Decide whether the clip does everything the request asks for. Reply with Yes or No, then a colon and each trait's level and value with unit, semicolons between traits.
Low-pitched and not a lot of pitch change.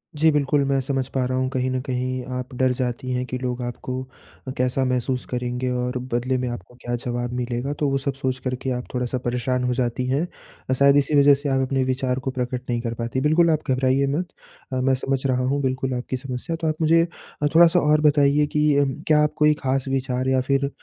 Yes: low, 130 Hz; narrow, 1.8 semitones